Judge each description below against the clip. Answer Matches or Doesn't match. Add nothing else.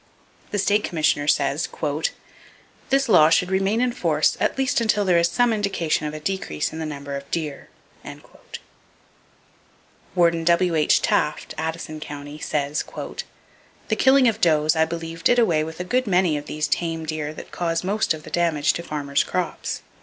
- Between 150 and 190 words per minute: Matches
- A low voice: Doesn't match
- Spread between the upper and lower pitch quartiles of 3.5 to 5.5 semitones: Matches